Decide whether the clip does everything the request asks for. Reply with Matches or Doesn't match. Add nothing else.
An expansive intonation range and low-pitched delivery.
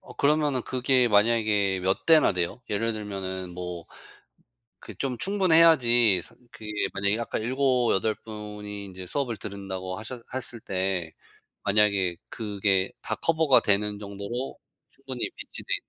Doesn't match